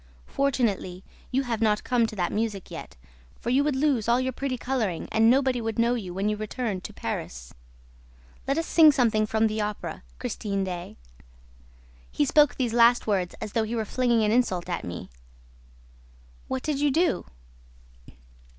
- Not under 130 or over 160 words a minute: No, average, 175 wpm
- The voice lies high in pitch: Yes, high, 225 Hz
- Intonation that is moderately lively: Yes, average, 3.7 semitones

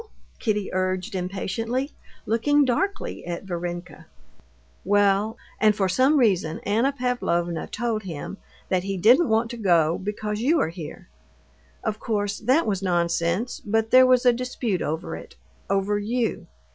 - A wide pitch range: No, average, 4.7 semitones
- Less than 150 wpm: Yes, average, 140 wpm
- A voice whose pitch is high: Yes, high, 210 Hz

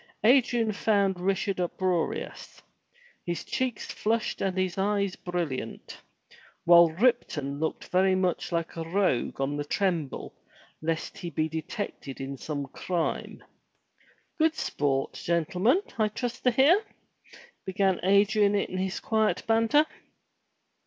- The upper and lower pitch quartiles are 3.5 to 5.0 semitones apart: Yes, average, 4.5 semitones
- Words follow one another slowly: Yes, slow, 120 wpm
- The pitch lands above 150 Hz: Yes, medium, 185 Hz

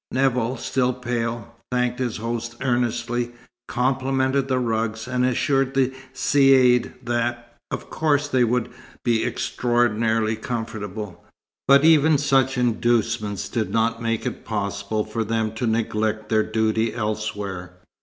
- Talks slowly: Yes, slow, 125 wpm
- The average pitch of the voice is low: Yes, low, 120 Hz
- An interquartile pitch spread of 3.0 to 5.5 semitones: No, narrow, 2.4 semitones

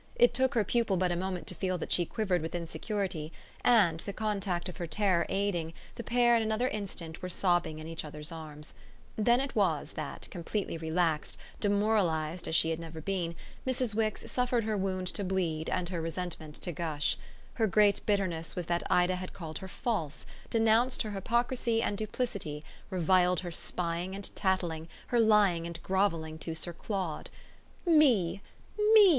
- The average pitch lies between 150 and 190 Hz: Yes, medium, 185 Hz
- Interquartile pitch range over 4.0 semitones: Yes, average, 4.4 semitones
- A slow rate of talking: No, average, 175 wpm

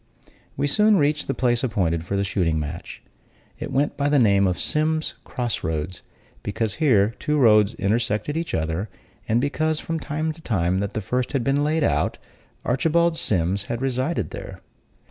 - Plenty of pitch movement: Yes, wide, 7.1 semitones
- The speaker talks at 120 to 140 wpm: No, average, 170 wpm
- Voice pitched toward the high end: No, low, 120 Hz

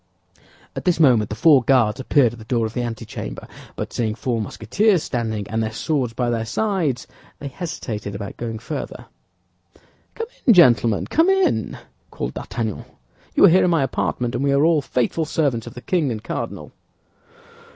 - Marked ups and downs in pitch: Yes, wide, 6.0 semitones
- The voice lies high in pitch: No, low, 125 Hz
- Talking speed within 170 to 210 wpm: Yes, average, 180 wpm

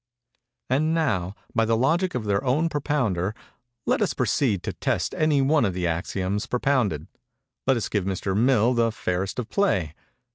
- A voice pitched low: Yes, low, 115 Hz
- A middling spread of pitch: No, wide, 6.4 semitones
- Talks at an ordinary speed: Yes, average, 170 wpm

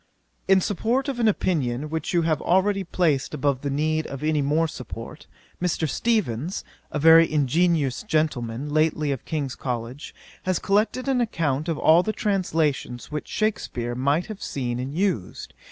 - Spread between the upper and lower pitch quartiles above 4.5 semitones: Yes, average, 5.1 semitones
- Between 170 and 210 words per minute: No, average, 160 wpm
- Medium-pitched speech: Yes, medium, 155 Hz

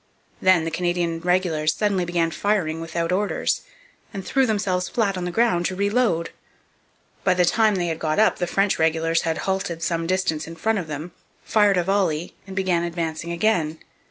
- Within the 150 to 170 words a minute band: No, average, 185 wpm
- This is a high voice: No, medium, 175 Hz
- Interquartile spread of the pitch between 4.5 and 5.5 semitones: No, average, 3.0 semitones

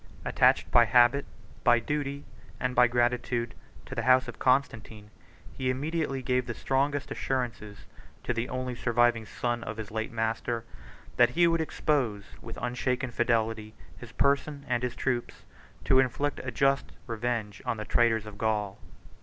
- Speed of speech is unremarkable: Yes, average, 160 wpm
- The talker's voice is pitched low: Yes, low, 120 Hz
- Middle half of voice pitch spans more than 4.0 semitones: No, average, 2.7 semitones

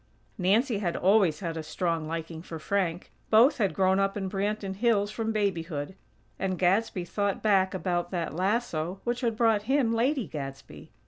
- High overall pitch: Yes, high, 195 Hz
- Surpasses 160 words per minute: Yes, average, 170 wpm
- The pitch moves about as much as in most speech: Yes, average, 4.0 semitones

